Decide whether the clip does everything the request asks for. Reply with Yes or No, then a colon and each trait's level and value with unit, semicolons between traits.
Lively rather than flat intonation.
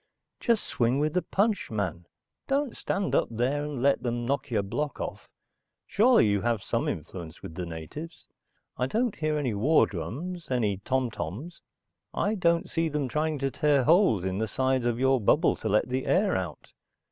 Yes: wide, 6.9 semitones